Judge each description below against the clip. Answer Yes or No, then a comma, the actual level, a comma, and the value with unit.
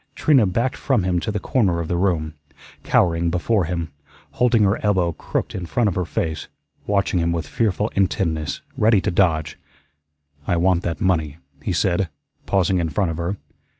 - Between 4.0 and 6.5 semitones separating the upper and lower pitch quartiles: No, average, 3.3 semitones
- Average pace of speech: Yes, average, 180 wpm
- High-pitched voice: No, very low, 90 Hz